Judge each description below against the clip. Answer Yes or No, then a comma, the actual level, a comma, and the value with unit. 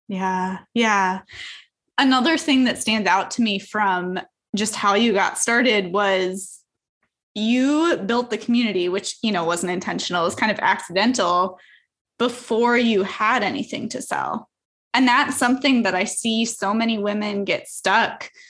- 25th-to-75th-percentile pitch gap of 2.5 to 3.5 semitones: No, average, 4.1 semitones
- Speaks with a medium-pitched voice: No, high, 215 Hz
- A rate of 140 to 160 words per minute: Yes, average, 150 wpm